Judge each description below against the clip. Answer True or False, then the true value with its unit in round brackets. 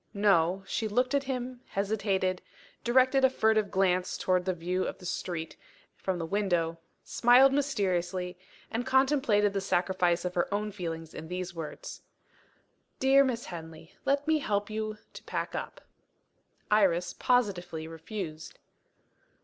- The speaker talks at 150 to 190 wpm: False (140 wpm)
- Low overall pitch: False (195 Hz)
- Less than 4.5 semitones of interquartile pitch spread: False (5.4 semitones)